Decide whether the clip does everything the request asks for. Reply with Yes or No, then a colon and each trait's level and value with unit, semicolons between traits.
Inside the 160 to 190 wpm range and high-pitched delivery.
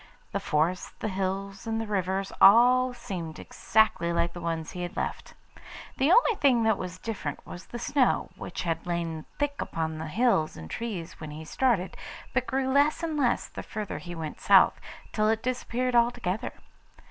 Yes: average, 180 wpm; high, 200 Hz